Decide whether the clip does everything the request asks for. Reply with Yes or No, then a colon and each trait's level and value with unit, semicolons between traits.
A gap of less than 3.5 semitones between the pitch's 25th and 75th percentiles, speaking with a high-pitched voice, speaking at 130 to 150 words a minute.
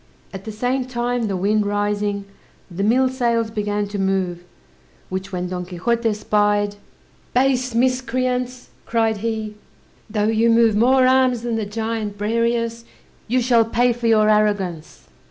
Yes: average, 2.7 semitones; high, 225 Hz; average, 145 wpm